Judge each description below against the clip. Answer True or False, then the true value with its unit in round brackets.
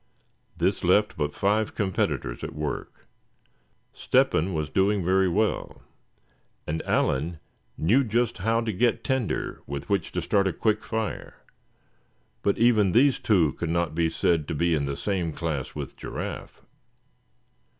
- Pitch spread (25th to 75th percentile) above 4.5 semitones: True (5.1 semitones)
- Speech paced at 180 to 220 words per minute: False (150 wpm)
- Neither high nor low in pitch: False (95 Hz)